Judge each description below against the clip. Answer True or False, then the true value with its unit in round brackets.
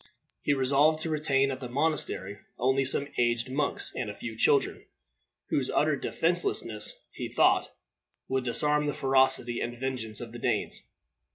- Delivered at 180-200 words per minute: False (155 wpm)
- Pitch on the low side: True (130 Hz)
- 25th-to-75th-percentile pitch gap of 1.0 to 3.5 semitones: True (3.1 semitones)